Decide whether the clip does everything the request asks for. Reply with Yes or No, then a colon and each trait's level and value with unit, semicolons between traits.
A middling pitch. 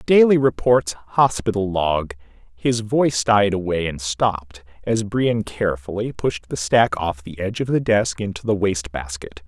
No: low, 100 Hz